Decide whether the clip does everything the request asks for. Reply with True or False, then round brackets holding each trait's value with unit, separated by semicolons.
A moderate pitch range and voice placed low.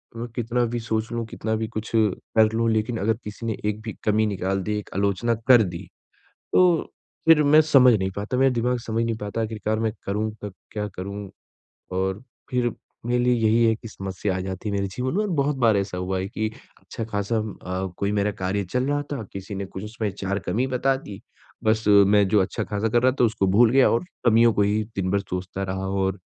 True (3.0 semitones; 110 Hz)